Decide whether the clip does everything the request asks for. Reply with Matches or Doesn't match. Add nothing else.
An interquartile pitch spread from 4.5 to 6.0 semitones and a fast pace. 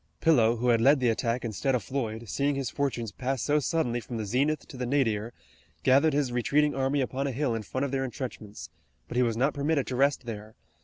Doesn't match